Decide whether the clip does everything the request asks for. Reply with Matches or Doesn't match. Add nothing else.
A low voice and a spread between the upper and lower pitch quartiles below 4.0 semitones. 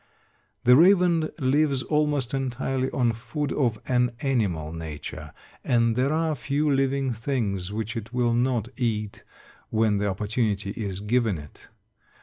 Doesn't match